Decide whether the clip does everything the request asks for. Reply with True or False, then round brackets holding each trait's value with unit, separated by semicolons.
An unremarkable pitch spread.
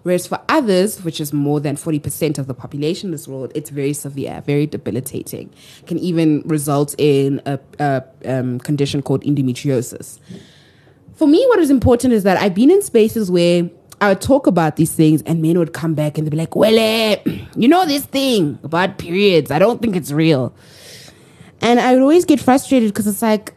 False (6.9 semitones)